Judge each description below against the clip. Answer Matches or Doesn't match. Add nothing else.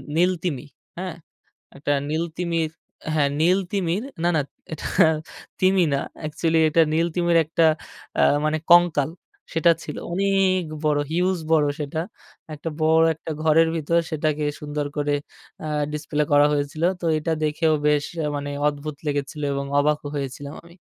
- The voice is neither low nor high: Matches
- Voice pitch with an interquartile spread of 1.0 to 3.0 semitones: Matches